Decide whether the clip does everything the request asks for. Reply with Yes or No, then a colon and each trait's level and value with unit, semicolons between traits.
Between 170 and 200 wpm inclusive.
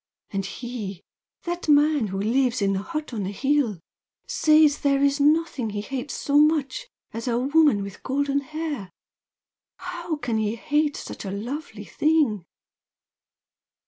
No: average, 145 wpm